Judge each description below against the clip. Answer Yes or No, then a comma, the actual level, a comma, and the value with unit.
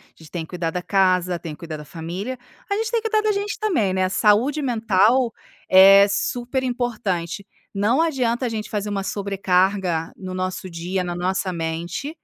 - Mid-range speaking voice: No, high, 195 Hz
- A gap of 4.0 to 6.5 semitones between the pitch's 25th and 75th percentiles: Yes, average, 5.2 semitones